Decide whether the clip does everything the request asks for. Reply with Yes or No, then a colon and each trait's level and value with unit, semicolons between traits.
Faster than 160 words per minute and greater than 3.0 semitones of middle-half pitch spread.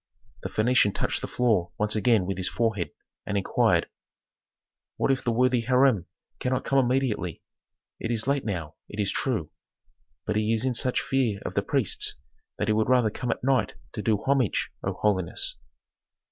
Yes: average, 175 wpm; average, 3.6 semitones